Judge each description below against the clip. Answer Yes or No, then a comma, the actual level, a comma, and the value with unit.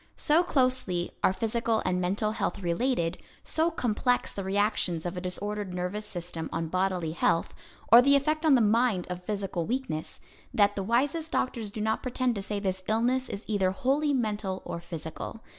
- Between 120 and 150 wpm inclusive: No, average, 175 wpm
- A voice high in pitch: Yes, high, 210 Hz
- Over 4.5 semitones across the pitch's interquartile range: Yes, wide, 5.4 semitones